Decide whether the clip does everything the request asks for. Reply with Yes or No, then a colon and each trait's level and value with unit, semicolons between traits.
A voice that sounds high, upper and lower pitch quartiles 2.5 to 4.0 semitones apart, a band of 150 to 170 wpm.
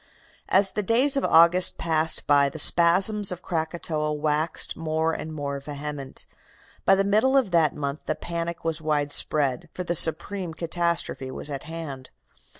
No: medium, 160 Hz; average, 3.0 semitones; average, 155 wpm